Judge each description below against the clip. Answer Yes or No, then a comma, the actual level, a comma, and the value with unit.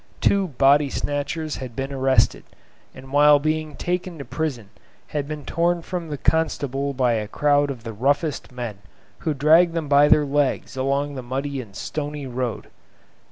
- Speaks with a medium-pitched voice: Yes, medium, 145 Hz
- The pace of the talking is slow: No, average, 165 wpm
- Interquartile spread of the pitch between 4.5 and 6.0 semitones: No, narrow, 2.6 semitones